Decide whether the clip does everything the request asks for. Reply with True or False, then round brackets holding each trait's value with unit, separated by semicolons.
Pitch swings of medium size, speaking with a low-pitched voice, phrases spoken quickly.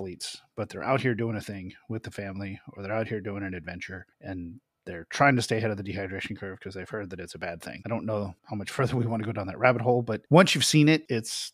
True (4.1 semitones; 110 Hz; 285 wpm)